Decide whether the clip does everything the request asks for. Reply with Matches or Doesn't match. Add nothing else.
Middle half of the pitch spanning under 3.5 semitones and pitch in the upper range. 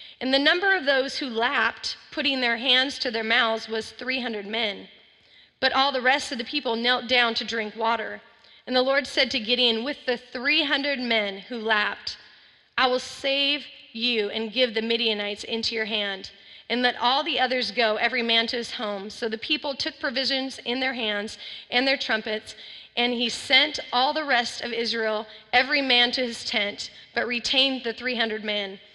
Matches